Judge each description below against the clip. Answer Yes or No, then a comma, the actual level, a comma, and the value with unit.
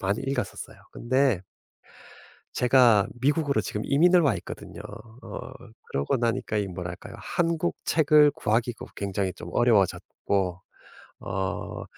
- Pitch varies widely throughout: Yes, wide, 6.1 semitones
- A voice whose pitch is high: No, low, 115 Hz